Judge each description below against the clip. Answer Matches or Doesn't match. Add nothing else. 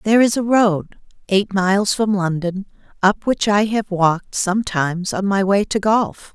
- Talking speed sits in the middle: Matches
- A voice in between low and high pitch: Doesn't match